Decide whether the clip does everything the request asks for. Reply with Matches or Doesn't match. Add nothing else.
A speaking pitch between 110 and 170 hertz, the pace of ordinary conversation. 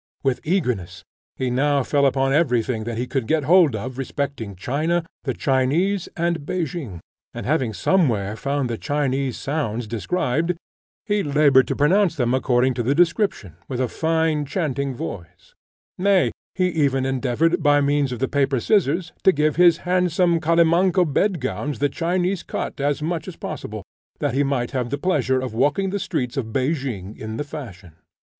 Matches